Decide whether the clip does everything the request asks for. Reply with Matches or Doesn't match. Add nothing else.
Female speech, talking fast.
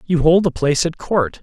Doesn't match